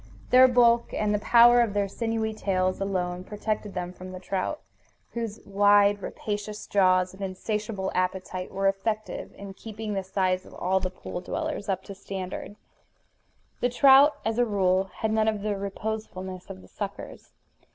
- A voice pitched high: Yes, high, 200 Hz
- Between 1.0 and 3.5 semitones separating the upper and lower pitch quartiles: Yes, average, 2.8 semitones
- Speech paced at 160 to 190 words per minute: Yes, average, 165 wpm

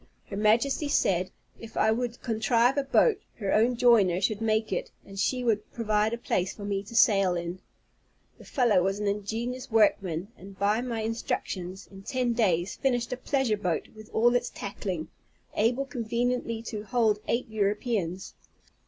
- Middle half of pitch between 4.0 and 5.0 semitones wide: No, average, 3.4 semitones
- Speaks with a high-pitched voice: Yes, high, 220 Hz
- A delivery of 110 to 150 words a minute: No, average, 170 wpm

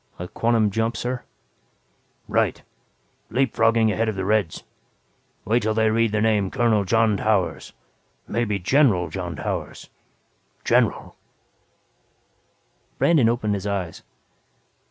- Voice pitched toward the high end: No, low, 110 Hz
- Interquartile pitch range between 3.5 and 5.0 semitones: No, narrow, 2.4 semitones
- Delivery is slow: Yes, slow, 115 wpm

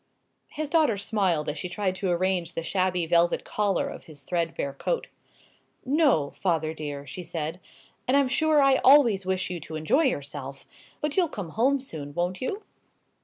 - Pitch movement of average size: No, wide, 8.4 semitones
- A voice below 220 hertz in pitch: Yes, medium, 185 Hz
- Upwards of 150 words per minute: Yes, average, 170 wpm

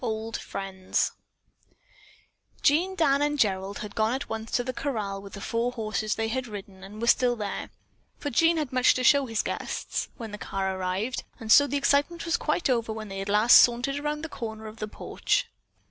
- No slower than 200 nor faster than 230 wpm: Yes, fast, 205 wpm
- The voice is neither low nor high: No, high, 225 Hz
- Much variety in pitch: No, average, 4.7 semitones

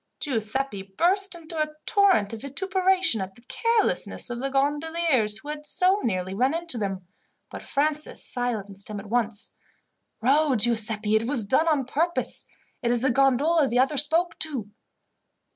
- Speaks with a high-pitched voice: Yes, very high, 270 Hz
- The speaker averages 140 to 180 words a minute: Yes, average, 160 wpm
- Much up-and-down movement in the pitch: Yes, wide, 6.3 semitones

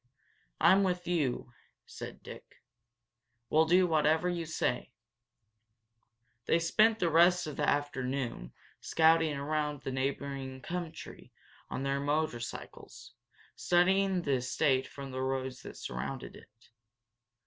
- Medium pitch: Yes, medium, 150 Hz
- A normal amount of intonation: Yes, average, 4.4 semitones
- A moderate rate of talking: No, slow, 115 wpm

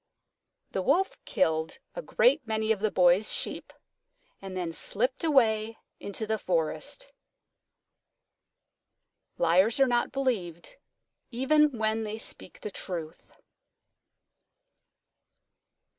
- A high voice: Yes, high, 220 Hz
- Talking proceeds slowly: Yes, slow, 100 wpm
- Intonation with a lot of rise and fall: Yes, wide, 5.9 semitones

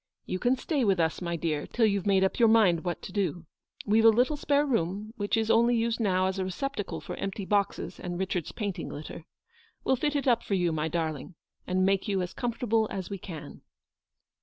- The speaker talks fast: Yes, fast, 220 wpm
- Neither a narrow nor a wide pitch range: Yes, average, 4.2 semitones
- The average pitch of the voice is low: No, high, 195 Hz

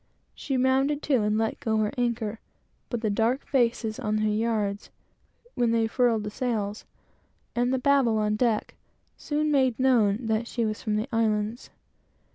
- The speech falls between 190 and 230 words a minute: No, average, 165 wpm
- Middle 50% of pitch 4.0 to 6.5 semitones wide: No, average, 2.9 semitones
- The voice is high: Yes, high, 230 Hz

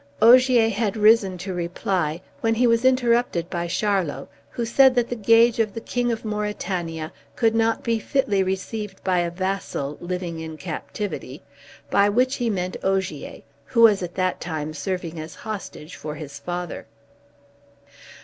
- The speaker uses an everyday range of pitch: Yes, average, 4.7 semitones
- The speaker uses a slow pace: No, average, 160 wpm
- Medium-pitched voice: No, high, 195 Hz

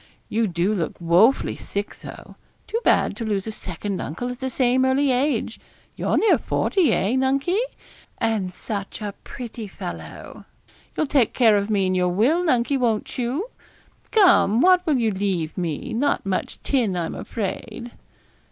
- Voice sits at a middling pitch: No, high, 225 Hz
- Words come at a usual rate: Yes, average, 160 wpm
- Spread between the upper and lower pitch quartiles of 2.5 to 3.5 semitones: No, average, 5.2 semitones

